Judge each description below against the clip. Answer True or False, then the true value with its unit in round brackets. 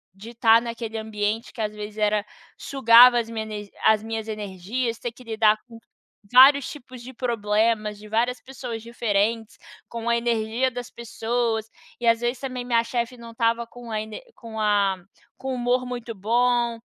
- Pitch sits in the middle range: False (230 Hz)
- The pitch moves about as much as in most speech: False (1.9 semitones)